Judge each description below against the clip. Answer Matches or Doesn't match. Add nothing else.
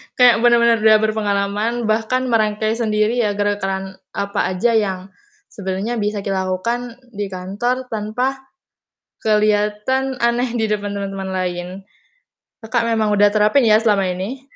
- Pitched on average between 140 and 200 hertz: Doesn't match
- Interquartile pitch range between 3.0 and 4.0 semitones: Doesn't match